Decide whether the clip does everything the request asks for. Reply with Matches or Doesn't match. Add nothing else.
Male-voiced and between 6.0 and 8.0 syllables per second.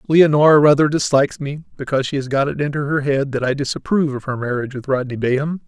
Matches